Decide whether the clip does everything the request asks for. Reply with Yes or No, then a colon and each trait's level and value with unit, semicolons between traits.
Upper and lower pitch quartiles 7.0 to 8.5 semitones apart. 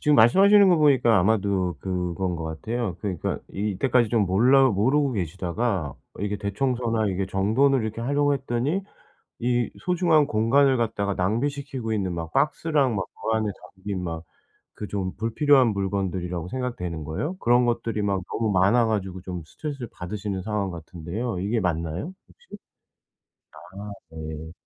No: average, 5.3 semitones